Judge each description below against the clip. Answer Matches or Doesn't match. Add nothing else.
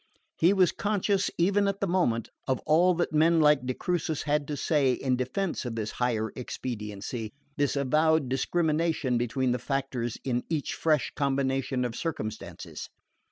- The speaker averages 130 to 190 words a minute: Matches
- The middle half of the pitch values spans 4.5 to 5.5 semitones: Matches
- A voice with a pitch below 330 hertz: Matches